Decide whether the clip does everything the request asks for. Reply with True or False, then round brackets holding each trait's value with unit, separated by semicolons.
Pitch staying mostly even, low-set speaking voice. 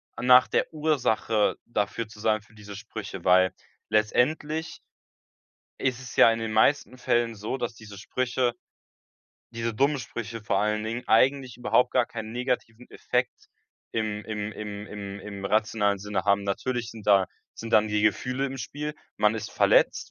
False (3.1 semitones; 110 Hz)